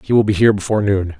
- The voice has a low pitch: Yes, low, 100 Hz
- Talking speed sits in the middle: No, fast, 305 wpm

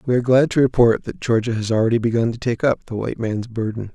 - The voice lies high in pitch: No, low, 115 Hz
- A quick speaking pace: Yes, fast, 260 wpm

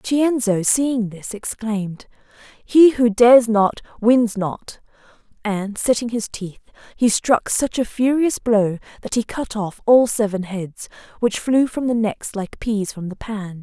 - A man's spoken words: No, female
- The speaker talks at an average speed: Yes, average, 165 wpm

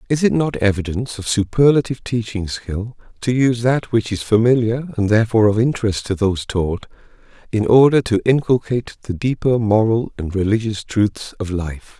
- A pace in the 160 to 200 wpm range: Yes, average, 165 wpm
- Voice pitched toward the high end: No, low, 110 Hz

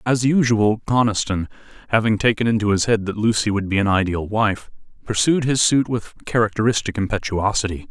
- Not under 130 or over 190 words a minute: Yes, average, 160 wpm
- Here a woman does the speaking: No, male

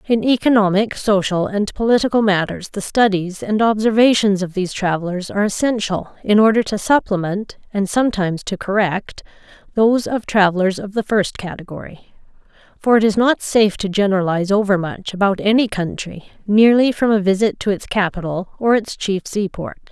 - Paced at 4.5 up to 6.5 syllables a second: Yes, 5.5 syllables/s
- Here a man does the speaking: No, female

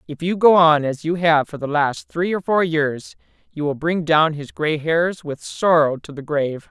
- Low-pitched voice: No, medium, 155 Hz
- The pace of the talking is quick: Yes, fast, 235 wpm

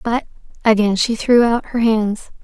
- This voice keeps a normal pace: Yes, average, 170 wpm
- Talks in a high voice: Yes, high, 225 Hz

